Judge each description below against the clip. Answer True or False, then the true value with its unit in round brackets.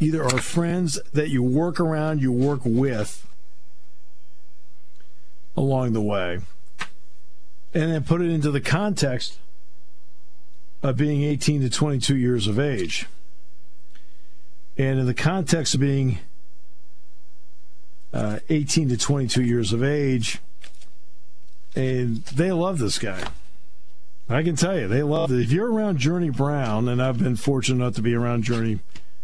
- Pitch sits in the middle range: False (120 Hz)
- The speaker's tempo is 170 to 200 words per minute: False (140 wpm)